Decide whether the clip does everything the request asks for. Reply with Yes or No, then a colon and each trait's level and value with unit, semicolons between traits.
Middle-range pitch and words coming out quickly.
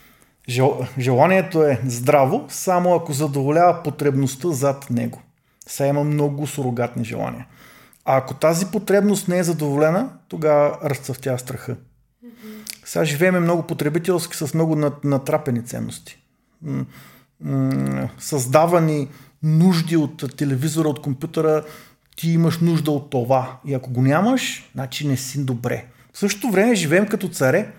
No: medium, 145 Hz; average, 125 wpm